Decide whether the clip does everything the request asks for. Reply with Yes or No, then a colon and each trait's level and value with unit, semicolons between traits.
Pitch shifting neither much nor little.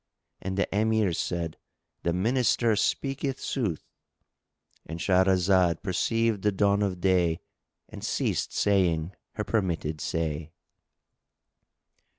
Yes: average, 3.8 semitones